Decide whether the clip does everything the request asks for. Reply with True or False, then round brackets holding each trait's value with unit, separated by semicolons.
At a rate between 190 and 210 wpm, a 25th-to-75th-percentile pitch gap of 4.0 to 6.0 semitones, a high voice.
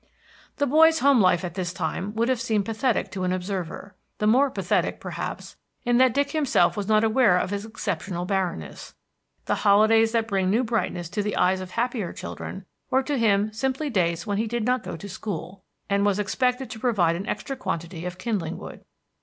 True (200 wpm; 4.5 semitones; 210 Hz)